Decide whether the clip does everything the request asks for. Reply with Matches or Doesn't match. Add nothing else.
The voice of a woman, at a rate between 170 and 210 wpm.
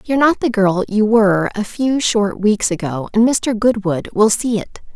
Matches